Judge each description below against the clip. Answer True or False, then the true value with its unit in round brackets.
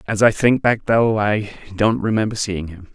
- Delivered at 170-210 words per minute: True (205 wpm)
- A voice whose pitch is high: False (105 Hz)